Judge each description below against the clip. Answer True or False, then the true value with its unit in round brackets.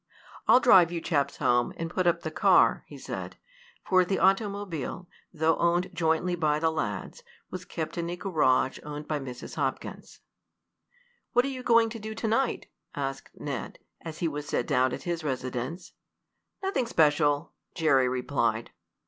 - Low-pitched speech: False (165 Hz)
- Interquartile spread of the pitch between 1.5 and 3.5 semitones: False (4.1 semitones)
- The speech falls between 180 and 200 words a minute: False (165 wpm)